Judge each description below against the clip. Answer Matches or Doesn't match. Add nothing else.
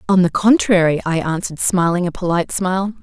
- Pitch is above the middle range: Doesn't match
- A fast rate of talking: Doesn't match